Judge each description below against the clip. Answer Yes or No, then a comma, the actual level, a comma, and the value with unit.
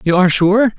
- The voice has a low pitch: No, high, 195 Hz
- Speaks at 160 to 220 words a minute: No, fast, 230 wpm